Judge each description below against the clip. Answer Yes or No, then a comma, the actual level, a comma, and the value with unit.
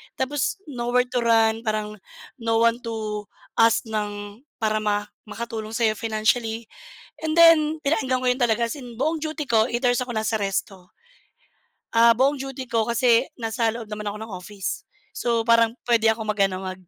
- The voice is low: No, high, 230 Hz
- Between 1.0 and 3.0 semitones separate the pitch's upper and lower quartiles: Yes, narrow, 2.4 semitones